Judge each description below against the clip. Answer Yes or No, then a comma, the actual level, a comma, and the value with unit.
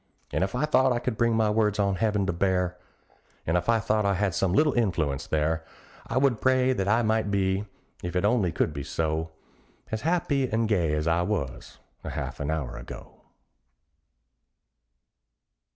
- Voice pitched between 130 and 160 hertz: No, low, 100 Hz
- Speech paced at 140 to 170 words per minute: No, average, 185 wpm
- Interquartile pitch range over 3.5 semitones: Yes, average, 5.0 semitones